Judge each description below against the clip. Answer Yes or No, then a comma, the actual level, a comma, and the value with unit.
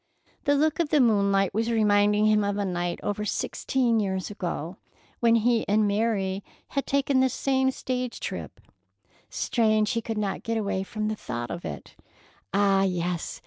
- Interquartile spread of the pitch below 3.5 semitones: Yes, average, 3.1 semitones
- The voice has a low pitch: No, high, 210 Hz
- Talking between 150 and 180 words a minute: Yes, average, 170 wpm